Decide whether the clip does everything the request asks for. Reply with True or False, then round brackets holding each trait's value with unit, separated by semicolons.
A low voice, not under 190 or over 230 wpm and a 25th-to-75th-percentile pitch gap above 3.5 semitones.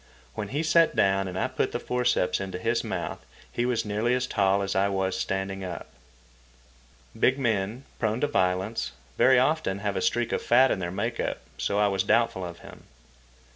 True (105 Hz; 195 wpm; 4.1 semitones)